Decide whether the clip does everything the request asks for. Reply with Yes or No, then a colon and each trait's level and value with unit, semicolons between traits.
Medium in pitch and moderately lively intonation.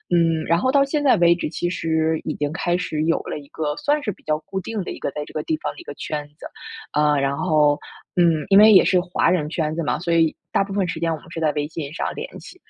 Yes: medium, 165 Hz; average, 3.9 semitones